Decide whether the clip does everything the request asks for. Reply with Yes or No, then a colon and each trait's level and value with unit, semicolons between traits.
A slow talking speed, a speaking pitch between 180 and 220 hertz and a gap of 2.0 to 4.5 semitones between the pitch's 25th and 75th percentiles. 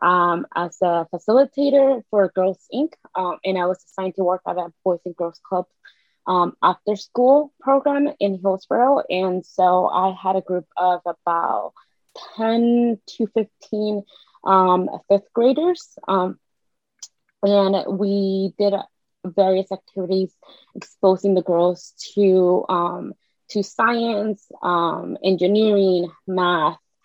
Yes: slow, 125 wpm; high, 190 Hz; average, 2.8 semitones